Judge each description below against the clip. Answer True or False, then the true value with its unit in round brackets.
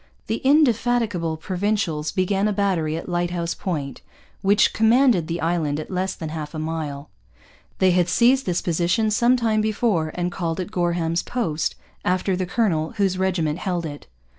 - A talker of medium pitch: True (180 Hz)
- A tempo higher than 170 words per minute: False (165 wpm)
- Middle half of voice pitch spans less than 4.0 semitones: False (4.3 semitones)